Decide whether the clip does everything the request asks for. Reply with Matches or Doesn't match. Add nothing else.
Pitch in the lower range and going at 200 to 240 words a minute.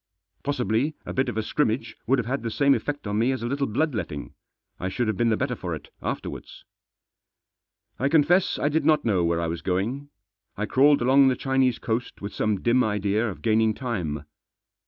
Matches